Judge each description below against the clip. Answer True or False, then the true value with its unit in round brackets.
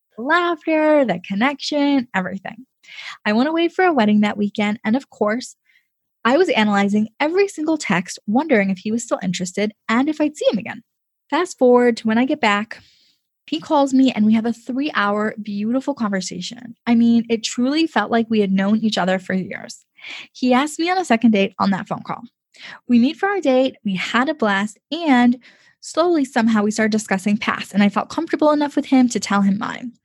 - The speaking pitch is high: True (235 Hz)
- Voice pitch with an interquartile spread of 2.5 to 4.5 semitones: False (5.2 semitones)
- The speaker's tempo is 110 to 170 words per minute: False (200 wpm)